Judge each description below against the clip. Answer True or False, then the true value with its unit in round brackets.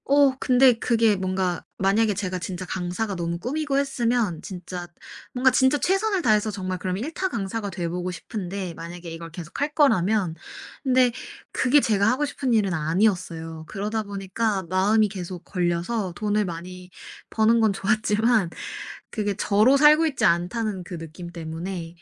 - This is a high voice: True (200 Hz)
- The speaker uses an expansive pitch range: False (4.6 semitones)